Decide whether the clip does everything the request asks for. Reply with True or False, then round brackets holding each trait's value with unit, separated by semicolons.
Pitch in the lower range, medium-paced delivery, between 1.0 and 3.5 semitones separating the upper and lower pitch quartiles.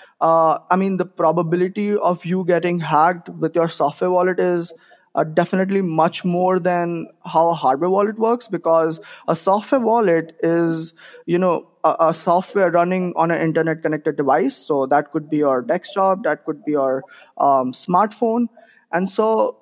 False (175 Hz; 165 wpm; 2.6 semitones)